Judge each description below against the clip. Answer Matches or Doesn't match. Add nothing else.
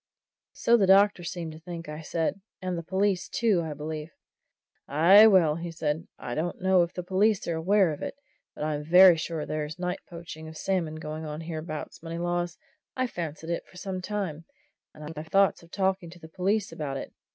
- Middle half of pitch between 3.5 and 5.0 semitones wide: Doesn't match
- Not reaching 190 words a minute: Doesn't match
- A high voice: Doesn't match